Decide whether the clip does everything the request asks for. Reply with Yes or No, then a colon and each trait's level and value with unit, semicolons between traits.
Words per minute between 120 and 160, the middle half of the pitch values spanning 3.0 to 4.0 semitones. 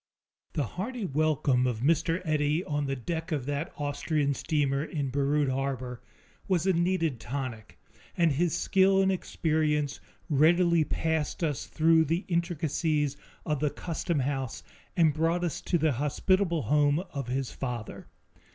Yes: average, 140 wpm; average, 3.3 semitones